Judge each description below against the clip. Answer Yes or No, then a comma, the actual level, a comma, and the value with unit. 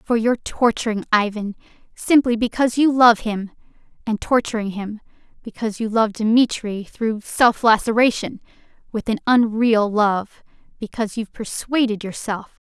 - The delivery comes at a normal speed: No, slow, 115 wpm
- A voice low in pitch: No, high, 225 Hz